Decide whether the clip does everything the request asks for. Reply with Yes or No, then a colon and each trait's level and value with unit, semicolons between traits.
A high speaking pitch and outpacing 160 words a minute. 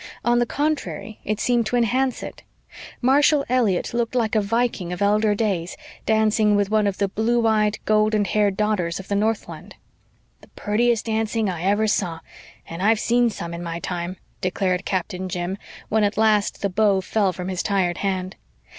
Yes: high, 210 Hz; average, 180 wpm